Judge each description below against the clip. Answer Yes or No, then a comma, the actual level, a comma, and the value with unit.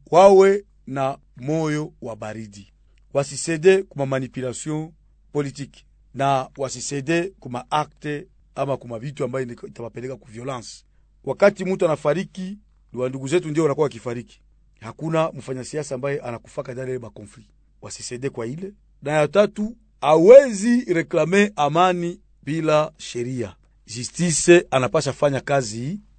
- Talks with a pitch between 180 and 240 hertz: No, medium, 140 Hz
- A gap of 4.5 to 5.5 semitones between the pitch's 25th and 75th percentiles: Yes, average, 5.1 semitones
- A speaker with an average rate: No, slow, 110 wpm